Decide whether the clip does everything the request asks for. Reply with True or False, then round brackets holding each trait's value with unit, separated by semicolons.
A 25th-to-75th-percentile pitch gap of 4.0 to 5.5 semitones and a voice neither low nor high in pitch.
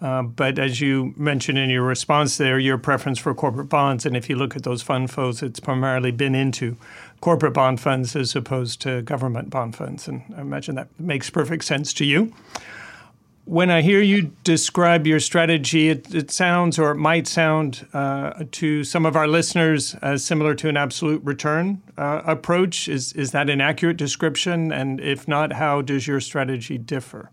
False (2.9 semitones; 145 Hz)